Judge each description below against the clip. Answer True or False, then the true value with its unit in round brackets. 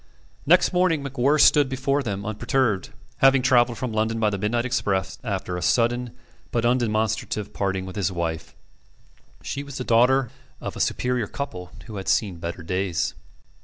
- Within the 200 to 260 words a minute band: False (165 wpm)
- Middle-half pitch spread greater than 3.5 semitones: True (4.9 semitones)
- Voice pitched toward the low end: True (115 Hz)